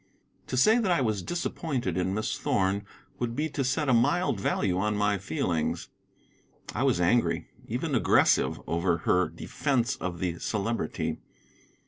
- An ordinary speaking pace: Yes, average, 150 wpm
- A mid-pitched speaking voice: No, low, 105 Hz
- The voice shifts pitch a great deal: Yes, wide, 5.9 semitones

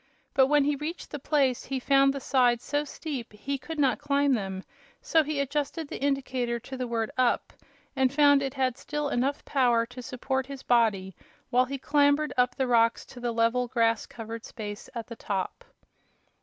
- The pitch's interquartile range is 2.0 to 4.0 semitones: Yes, average, 3.1 semitones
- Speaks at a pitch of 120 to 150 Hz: No, very high, 260 Hz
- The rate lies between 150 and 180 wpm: No, average, 195 wpm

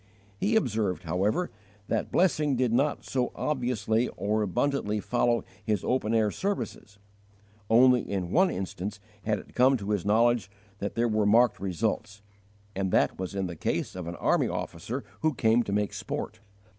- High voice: No, low, 110 Hz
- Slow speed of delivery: No, average, 165 wpm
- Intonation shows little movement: No, average, 3.8 semitones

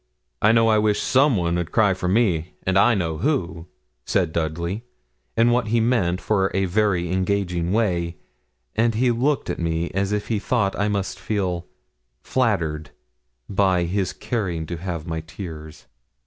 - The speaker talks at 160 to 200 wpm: Yes, average, 165 wpm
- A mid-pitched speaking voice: No, very low, 95 Hz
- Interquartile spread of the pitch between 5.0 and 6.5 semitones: No, average, 4.1 semitones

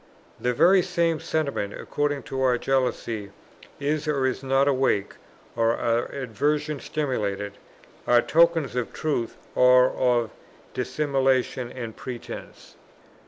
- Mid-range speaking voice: No, low, 130 Hz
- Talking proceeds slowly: Yes, slow, 120 wpm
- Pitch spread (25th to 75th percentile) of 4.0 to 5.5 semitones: No, average, 3.5 semitones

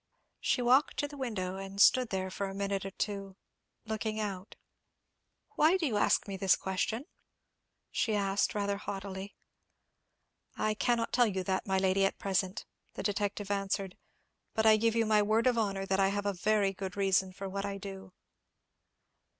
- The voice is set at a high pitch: Yes, high, 200 Hz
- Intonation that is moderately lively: No, narrow, 2.0 semitones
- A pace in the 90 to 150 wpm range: No, average, 175 wpm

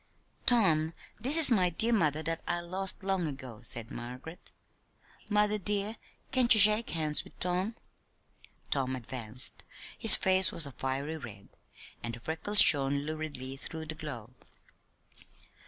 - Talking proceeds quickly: No, average, 140 wpm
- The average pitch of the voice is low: No, medium, 160 Hz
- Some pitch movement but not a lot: No, wide, 6.5 semitones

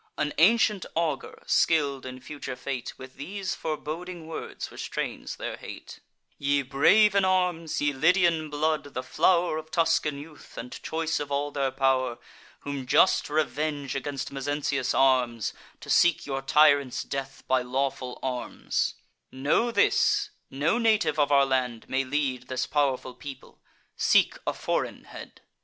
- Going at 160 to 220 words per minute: No, average, 145 wpm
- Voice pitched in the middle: Yes, medium, 145 Hz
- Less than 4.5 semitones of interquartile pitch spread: Yes, average, 3.2 semitones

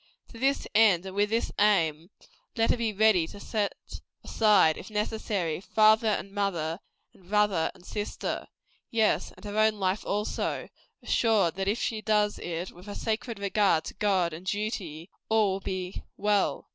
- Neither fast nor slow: Yes, average, 170 wpm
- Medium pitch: No, high, 205 Hz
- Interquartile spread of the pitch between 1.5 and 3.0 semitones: Yes, average, 2.7 semitones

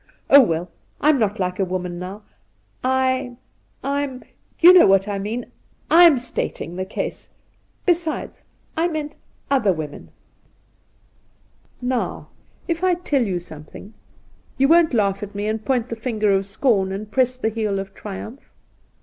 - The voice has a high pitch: Yes, high, 220 Hz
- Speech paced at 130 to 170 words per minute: Yes, average, 155 wpm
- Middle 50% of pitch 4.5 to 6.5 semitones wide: Yes, wide, 5.6 semitones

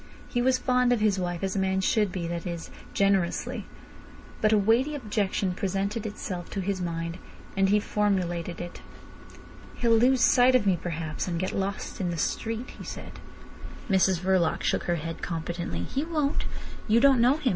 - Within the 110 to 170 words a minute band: No, average, 180 wpm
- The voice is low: No, high, 195 Hz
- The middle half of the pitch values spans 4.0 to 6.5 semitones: Yes, average, 4.7 semitones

